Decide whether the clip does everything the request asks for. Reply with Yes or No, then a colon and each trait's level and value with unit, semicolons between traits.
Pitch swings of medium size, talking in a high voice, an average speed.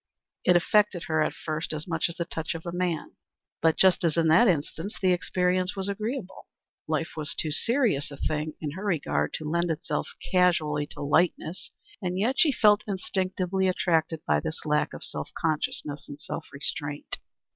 No: average, 3.3 semitones; medium, 170 Hz; average, 175 wpm